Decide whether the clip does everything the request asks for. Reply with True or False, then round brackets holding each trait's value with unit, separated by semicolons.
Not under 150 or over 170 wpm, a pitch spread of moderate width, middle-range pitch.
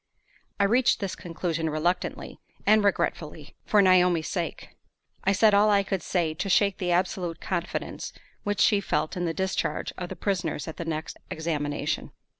True (165 wpm; 3.5 semitones; 180 Hz)